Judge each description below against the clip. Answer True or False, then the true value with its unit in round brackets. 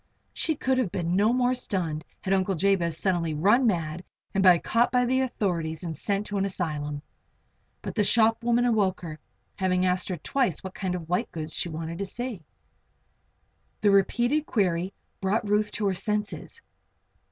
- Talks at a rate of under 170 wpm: False (175 wpm)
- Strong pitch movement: False (4.6 semitones)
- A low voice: False (195 Hz)